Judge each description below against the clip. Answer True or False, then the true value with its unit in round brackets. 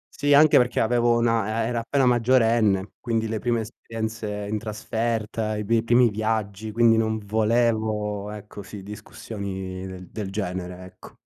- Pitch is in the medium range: False (110 Hz)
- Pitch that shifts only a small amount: True (2.1 semitones)